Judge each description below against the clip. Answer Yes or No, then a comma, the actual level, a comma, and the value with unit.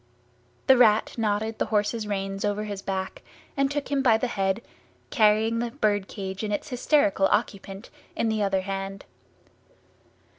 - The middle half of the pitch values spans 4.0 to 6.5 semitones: No, average, 2.8 semitones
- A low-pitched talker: No, high, 210 Hz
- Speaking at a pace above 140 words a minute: Yes, average, 155 wpm